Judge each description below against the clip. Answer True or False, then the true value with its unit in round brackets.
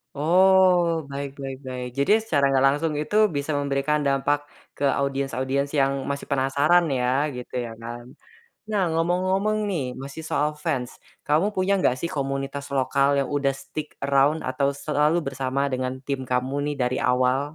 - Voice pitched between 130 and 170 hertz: True (140 Hz)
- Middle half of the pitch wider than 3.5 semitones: False (2.7 semitones)